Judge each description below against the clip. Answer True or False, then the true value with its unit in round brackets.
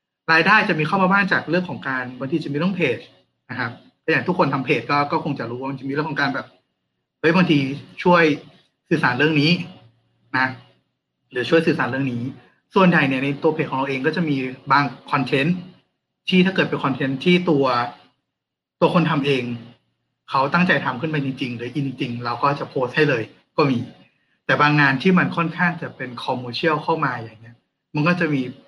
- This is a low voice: False (145 Hz)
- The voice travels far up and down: False (3.9 semitones)